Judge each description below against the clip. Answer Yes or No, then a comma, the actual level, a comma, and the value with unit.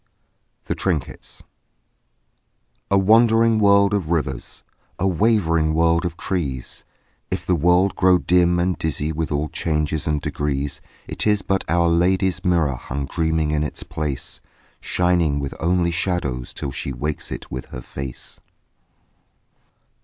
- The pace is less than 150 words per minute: Yes, average, 140 wpm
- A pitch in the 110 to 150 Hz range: No, very low, 85 Hz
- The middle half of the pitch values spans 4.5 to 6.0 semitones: No, average, 3.7 semitones